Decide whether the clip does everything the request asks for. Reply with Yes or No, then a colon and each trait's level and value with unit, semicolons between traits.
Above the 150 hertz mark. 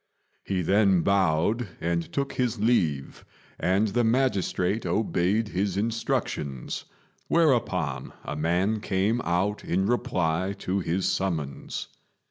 No: very low, 95 Hz